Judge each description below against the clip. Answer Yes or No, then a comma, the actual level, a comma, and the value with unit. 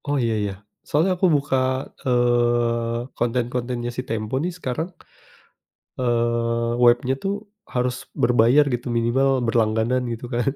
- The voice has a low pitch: Yes, low, 120 Hz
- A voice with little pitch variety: Yes, narrow, 1.5 semitones